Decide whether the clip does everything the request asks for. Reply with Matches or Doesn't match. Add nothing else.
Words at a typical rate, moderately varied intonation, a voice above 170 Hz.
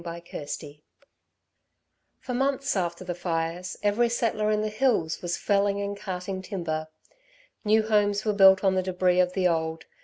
Matches